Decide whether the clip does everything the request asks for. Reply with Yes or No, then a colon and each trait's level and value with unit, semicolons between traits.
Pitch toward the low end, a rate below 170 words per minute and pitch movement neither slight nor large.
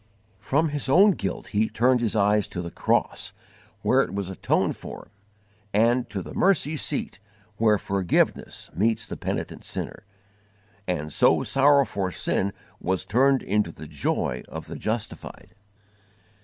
No: low, 105 Hz; average, 145 wpm; wide, 5.7 semitones